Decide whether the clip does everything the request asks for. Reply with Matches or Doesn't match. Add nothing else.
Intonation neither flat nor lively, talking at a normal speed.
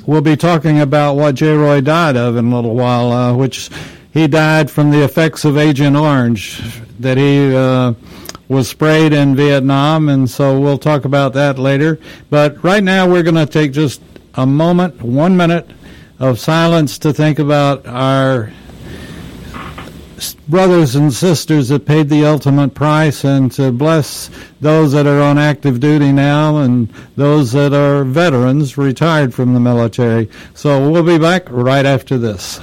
Matches